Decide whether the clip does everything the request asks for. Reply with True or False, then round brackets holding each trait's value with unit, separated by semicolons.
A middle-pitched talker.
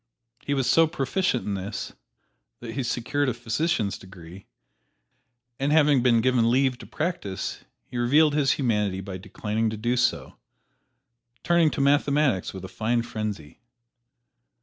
False (120 Hz)